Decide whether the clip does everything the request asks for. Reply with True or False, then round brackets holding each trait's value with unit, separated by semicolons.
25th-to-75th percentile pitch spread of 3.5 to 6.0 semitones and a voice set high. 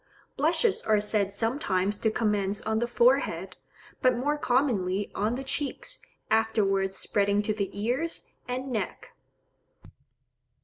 True (4.1 semitones; 220 Hz)